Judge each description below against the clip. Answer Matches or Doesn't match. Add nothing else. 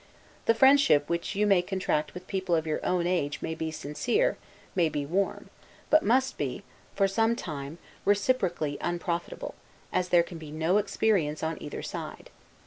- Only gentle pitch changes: Doesn't match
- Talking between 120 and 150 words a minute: Doesn't match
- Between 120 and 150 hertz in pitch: Doesn't match